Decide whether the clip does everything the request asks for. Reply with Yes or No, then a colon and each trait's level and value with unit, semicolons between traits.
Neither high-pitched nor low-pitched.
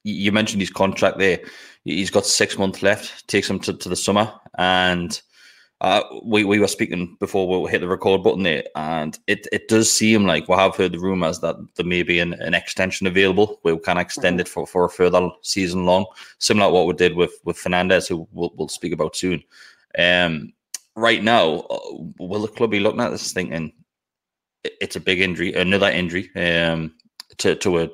No: very low, 90 Hz